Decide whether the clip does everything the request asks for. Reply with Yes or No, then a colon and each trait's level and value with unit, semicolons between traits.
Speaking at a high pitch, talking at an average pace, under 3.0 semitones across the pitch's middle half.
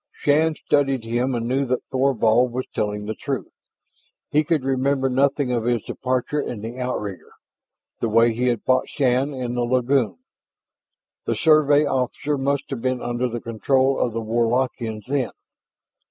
No: low, 125 Hz; average, 160 wpm; narrow, 2.6 semitones